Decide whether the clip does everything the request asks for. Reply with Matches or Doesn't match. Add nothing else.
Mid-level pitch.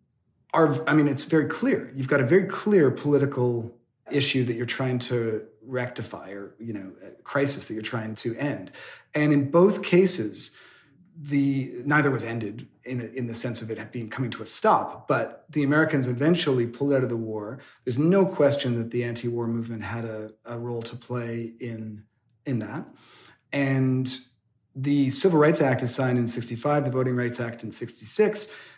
Doesn't match